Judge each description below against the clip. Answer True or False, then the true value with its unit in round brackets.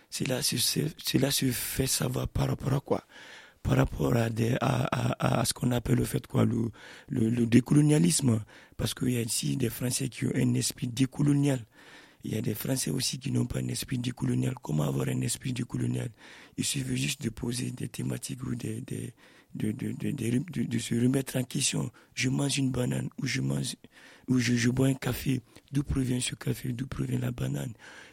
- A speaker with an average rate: True (205 wpm)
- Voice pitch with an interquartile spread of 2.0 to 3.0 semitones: True (2.5 semitones)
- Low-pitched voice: True (125 Hz)